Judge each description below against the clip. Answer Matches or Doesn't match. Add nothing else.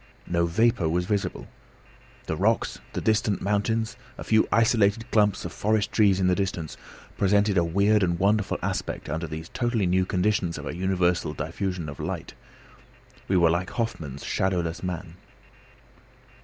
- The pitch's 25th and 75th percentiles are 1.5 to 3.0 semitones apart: Doesn't match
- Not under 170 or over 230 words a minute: Doesn't match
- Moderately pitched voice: Doesn't match